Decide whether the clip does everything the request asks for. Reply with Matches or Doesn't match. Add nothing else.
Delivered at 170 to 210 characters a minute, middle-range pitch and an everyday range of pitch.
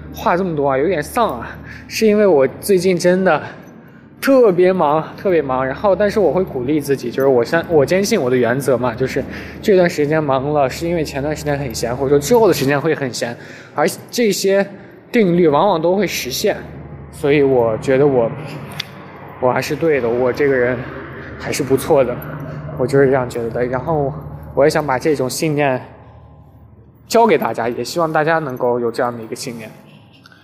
Doesn't match